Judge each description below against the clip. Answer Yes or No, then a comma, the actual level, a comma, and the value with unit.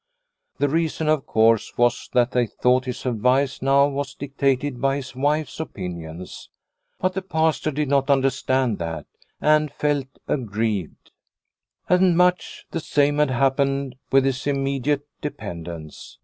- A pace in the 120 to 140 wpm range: Yes, slow, 135 wpm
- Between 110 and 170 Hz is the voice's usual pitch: Yes, low, 135 Hz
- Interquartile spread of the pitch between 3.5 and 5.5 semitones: No, average, 3.1 semitones